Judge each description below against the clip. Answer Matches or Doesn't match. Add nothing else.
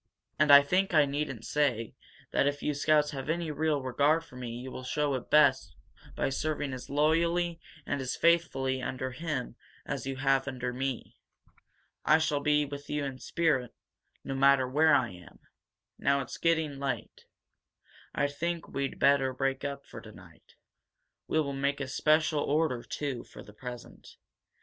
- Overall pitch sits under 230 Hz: Matches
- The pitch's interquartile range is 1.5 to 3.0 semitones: Matches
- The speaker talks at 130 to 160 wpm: Doesn't match